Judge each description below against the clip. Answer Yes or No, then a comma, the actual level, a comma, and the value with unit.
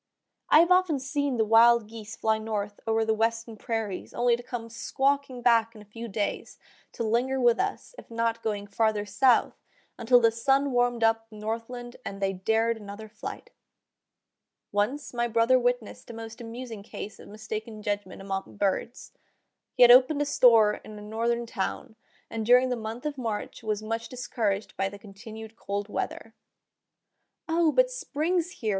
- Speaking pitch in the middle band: No, high, 230 Hz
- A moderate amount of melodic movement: No, narrow, 2.3 semitones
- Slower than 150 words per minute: No, average, 175 wpm